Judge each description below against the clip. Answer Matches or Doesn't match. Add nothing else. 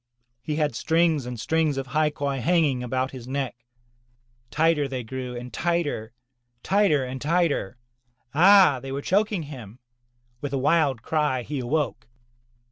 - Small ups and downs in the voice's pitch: Doesn't match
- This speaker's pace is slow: Doesn't match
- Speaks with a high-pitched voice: Doesn't match